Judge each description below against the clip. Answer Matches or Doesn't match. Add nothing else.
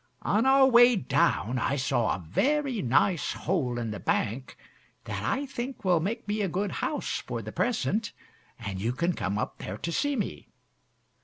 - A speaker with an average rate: Matches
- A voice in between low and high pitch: Matches